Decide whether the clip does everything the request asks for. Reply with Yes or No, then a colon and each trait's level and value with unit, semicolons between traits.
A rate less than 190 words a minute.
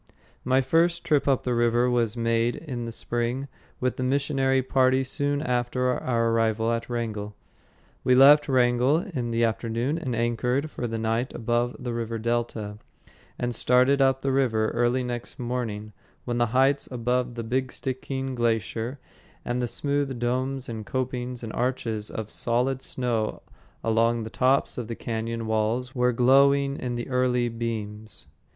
Yes: average, 160 wpm